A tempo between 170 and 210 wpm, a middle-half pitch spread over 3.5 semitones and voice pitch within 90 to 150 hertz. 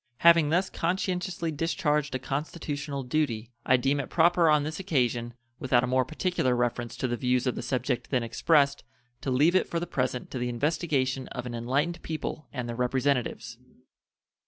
Yes: average, 180 wpm; average, 4.2 semitones; medium, 140 Hz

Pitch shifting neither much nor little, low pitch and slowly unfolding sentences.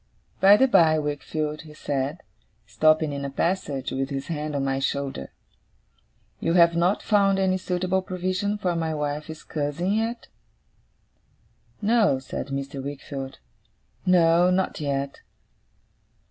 No: average, 4.8 semitones; medium, 155 Hz; slow, 130 wpm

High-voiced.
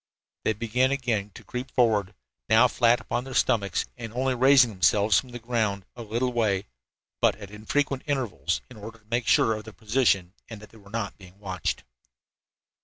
No: low, 115 Hz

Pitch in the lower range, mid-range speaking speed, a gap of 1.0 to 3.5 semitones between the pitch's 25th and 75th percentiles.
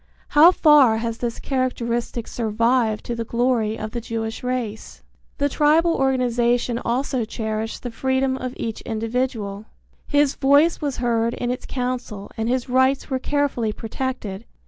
No: high, 245 Hz; average, 145 wpm; average, 2.7 semitones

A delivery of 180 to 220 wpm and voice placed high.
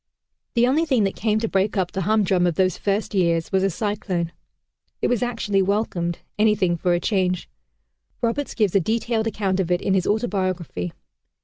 Yes: average, 185 wpm; high, 195 Hz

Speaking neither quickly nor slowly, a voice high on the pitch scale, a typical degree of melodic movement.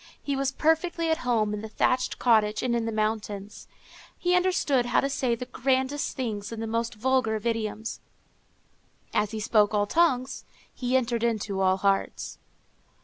Yes: average, 170 wpm; high, 235 Hz; average, 3.6 semitones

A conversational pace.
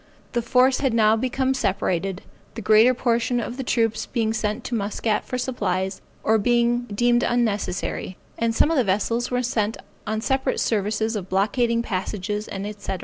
Yes: average, 160 wpm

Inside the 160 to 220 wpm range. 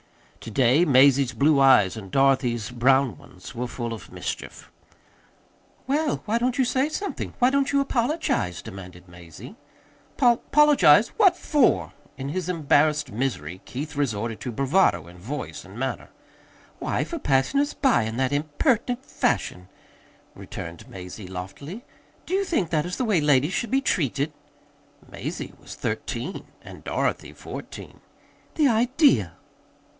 No: average, 145 wpm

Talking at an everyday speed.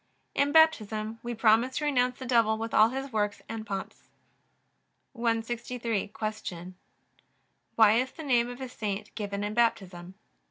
Yes: average, 150 wpm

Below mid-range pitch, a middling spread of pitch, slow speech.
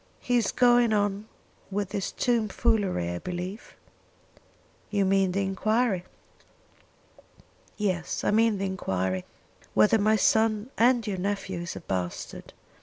No: high, 205 Hz; average, 3.1 semitones; slow, 130 wpm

